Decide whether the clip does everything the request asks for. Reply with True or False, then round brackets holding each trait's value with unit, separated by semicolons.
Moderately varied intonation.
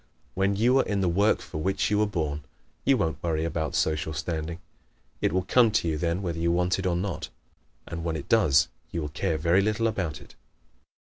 True (3.8 semitones)